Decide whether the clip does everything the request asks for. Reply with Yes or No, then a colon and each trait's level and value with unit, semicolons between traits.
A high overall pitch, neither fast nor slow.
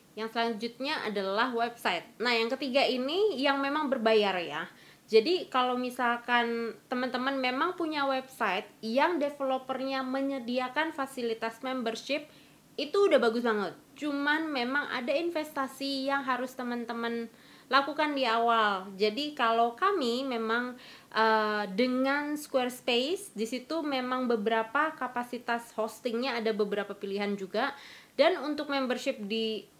Yes: very high, 250 Hz; average, 120 wpm